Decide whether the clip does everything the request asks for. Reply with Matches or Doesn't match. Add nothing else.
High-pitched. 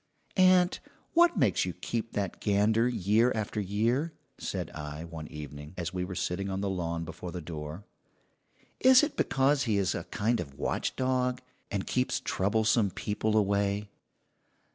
Doesn't match